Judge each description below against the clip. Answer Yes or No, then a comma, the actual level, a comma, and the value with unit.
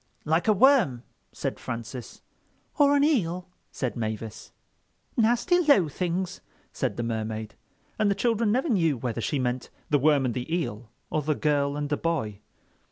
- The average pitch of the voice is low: No, medium, 150 Hz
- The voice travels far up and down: Yes, wide, 9.0 semitones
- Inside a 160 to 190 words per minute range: Yes, average, 165 wpm